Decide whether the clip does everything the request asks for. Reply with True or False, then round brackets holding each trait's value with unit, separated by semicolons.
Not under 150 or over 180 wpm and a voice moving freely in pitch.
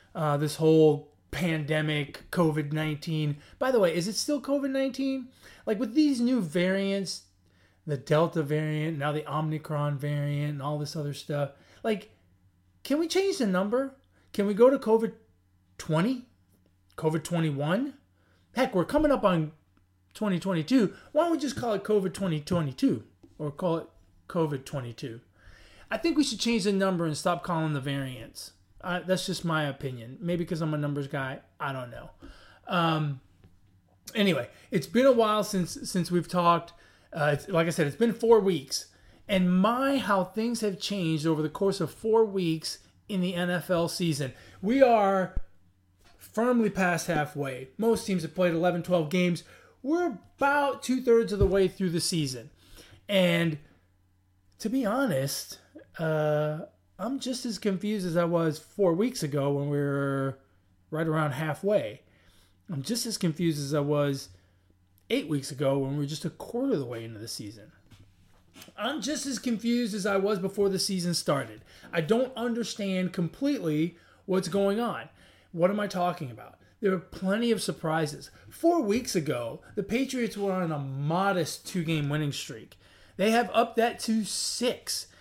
True (165 wpm; 6.4 semitones)